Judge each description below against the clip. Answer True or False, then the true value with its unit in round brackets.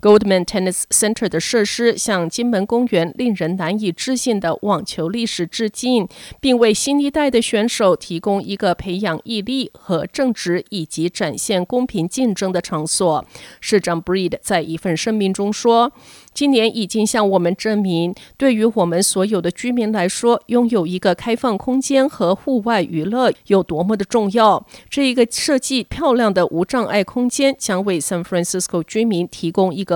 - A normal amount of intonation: True (4.8 semitones)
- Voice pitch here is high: True (210 Hz)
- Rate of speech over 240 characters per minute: True (315 characters per minute)